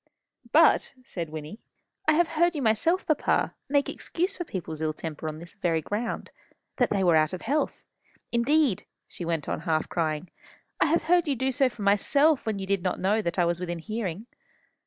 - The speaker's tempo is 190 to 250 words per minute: Yes, average, 200 wpm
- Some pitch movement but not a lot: No, wide, 8.8 semitones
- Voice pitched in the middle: No, high, 200 Hz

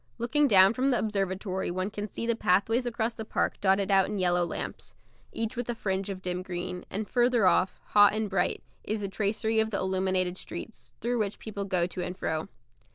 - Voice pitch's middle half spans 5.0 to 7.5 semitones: No, average, 3.1 semitones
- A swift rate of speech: Yes, fast, 215 wpm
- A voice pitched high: Yes, high, 200 Hz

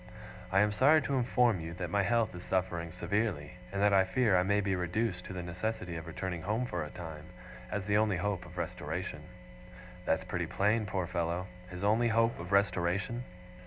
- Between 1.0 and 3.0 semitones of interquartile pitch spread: No, average, 3.4 semitones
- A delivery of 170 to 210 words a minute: Yes, average, 200 wpm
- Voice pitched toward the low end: Yes, very low, 95 Hz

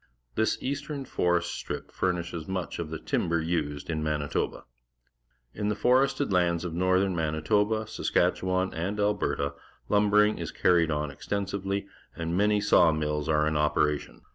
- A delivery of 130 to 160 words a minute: Yes, average, 140 wpm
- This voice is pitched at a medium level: No, very low, 90 Hz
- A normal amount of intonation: Yes, average, 4.7 semitones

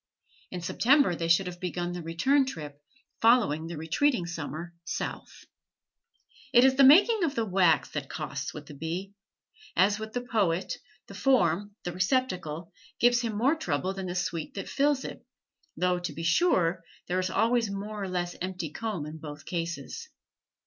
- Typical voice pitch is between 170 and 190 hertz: Yes, medium, 185 Hz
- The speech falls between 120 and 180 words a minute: Yes, average, 170 wpm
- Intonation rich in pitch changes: Yes, wide, 5.9 semitones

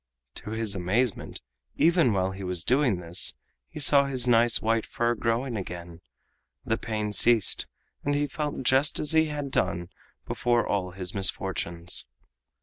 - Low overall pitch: Yes, low, 115 Hz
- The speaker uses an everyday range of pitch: No, wide, 5.8 semitones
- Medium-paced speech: Yes, average, 150 wpm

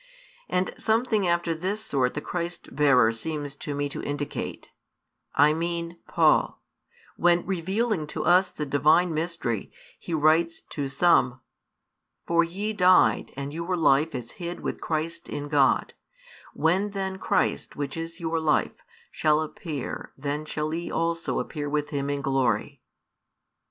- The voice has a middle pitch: Yes, medium, 160 Hz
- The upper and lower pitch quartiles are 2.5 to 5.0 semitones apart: Yes, average, 3.2 semitones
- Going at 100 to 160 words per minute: Yes, average, 145 wpm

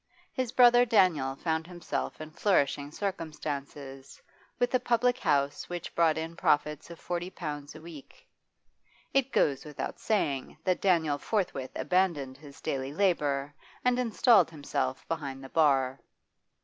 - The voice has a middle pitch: Yes, medium, 155 Hz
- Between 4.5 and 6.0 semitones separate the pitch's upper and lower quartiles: Yes, average, 4.9 semitones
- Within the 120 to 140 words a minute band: Yes, slow, 135 wpm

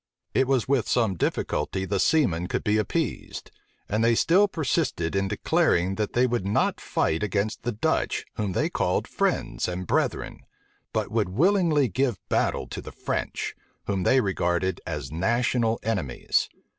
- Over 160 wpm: No, average, 155 wpm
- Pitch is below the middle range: Yes, low, 105 Hz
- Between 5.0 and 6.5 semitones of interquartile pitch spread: Yes, average, 5.3 semitones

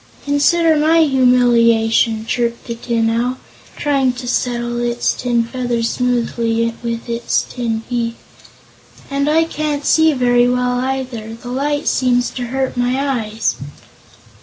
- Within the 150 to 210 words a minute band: No, slow, 135 wpm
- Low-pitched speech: No, high, 245 Hz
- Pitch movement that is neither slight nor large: No, narrow, 2.3 semitones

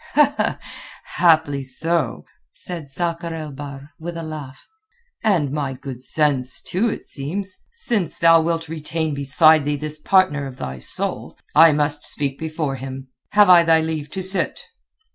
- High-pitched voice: No, medium, 155 Hz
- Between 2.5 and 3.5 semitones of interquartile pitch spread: Yes, average, 3.1 semitones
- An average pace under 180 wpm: Yes, average, 150 wpm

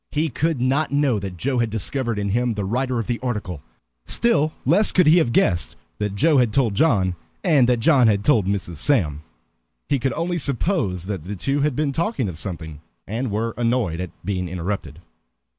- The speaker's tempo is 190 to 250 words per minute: Yes, average, 195 wpm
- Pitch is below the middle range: Yes, low, 120 Hz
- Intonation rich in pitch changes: Yes, wide, 6.3 semitones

